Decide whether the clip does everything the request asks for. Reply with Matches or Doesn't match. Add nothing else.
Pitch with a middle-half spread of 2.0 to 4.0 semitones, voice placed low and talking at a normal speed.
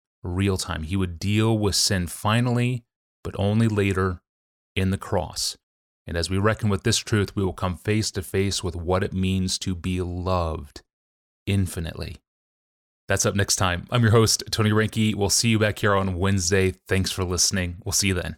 Matches